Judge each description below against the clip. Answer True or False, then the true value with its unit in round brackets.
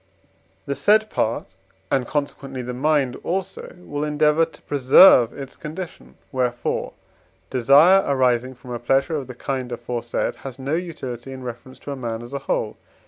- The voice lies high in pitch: False (135 Hz)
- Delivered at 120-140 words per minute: False (160 wpm)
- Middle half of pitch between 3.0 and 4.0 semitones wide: True (3.4 semitones)